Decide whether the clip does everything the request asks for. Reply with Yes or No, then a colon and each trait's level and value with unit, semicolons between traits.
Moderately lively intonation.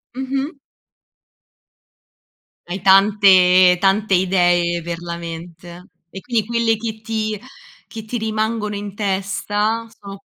Yes: average, 3.4 semitones